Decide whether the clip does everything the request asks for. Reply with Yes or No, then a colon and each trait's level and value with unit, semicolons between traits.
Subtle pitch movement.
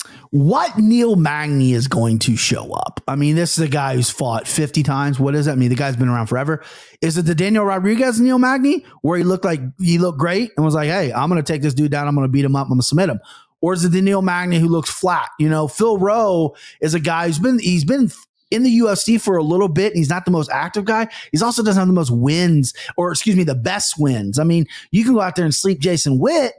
No: average, 5.1 semitones